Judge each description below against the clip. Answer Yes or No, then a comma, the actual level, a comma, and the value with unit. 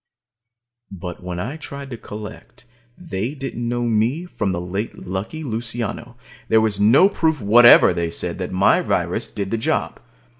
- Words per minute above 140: Yes, average, 160 wpm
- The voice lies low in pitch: Yes, low, 115 Hz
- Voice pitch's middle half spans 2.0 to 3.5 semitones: No, average, 4.5 semitones